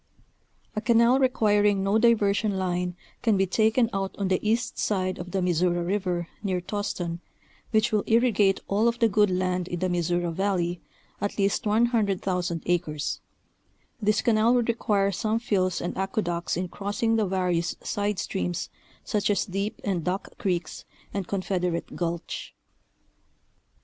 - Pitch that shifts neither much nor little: Yes, average, 3.1 semitones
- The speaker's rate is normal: Yes, average, 150 wpm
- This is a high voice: Yes, high, 195 Hz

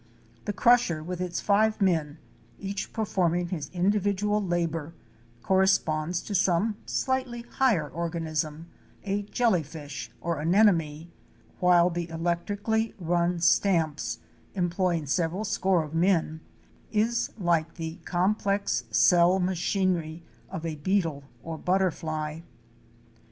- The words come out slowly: Yes, slow, 110 wpm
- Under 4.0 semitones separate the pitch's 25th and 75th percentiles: Yes, average, 3.5 semitones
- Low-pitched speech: No, medium, 175 Hz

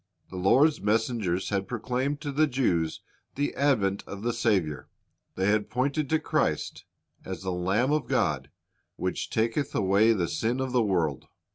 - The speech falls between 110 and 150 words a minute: No, average, 160 wpm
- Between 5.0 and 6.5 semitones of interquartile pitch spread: Yes, wide, 5.5 semitones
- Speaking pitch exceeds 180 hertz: No, low, 110 Hz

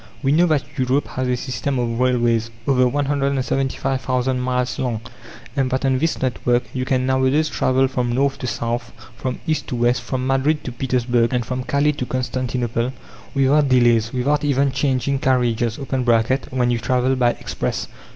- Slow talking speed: No, average, 165 wpm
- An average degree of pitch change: No, narrow, 1.7 semitones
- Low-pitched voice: Yes, low, 130 Hz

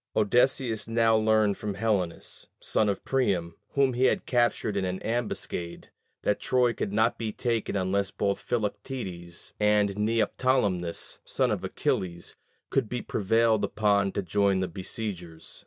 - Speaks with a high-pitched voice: No, low, 105 Hz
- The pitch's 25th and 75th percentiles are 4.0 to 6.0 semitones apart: No, average, 3.1 semitones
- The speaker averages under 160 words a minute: Yes, average, 140 wpm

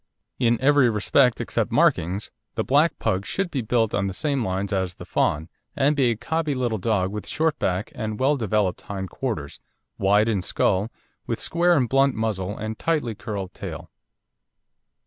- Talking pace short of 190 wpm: Yes, average, 175 wpm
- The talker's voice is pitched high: No, low, 110 Hz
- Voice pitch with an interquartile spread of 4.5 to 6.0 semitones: Yes, wide, 5.6 semitones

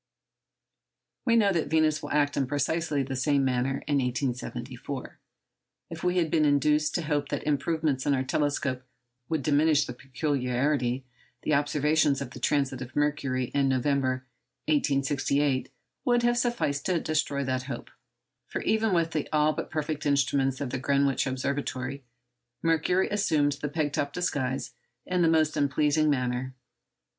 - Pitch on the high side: No, medium, 145 Hz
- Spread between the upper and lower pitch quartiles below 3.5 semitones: Yes, average, 2.7 semitones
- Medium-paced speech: Yes, average, 150 wpm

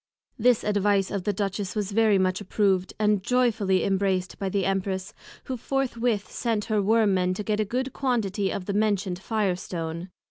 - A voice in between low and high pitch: No, high, 205 Hz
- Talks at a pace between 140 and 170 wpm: No, average, 180 wpm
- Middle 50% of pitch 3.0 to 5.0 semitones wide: No, narrow, 2.4 semitones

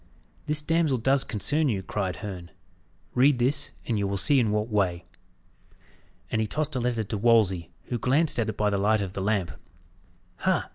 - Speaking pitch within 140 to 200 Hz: No, low, 110 Hz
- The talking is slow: No, average, 190 wpm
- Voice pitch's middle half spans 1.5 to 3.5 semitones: No, average, 5.1 semitones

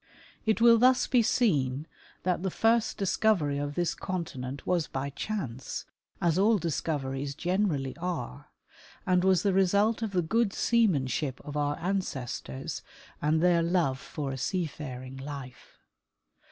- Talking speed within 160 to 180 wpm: No, average, 140 wpm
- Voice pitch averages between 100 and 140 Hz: No, medium, 170 Hz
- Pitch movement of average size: No, wide, 6.0 semitones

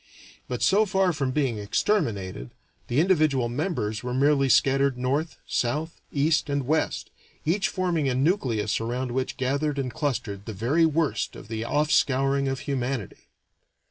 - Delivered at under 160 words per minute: Yes, average, 145 wpm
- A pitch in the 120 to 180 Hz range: Yes, low, 135 Hz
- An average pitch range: Yes, average, 4.1 semitones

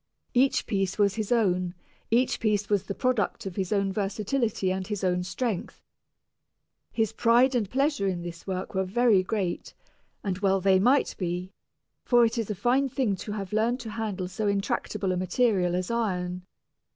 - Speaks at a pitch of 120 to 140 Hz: No, high, 200 Hz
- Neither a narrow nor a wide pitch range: Yes, average, 3.7 semitones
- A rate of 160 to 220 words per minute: Yes, average, 175 wpm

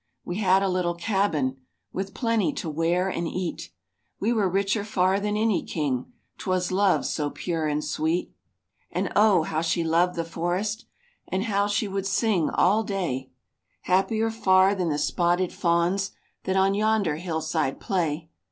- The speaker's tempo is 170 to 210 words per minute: No, average, 160 wpm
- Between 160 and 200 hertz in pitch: Yes, medium, 185 Hz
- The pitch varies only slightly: No, average, 3.3 semitones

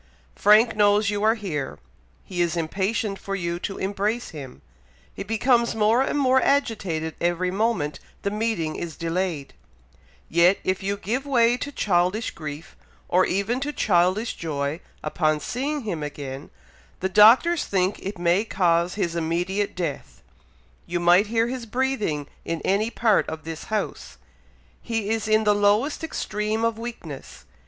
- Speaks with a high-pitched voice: Yes, high, 200 Hz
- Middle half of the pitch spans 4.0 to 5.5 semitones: Yes, average, 4.7 semitones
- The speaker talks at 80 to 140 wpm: No, average, 150 wpm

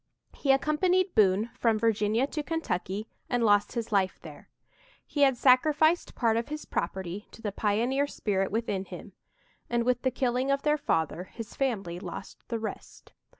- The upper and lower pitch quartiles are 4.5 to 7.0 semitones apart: Yes, average, 5.0 semitones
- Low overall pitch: No, high, 235 Hz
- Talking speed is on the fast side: No, average, 165 wpm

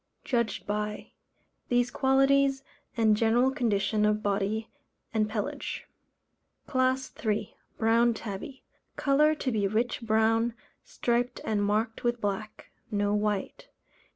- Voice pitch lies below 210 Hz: No, high, 225 Hz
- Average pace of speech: No, slow, 115 wpm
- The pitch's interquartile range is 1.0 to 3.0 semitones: Yes, average, 2.7 semitones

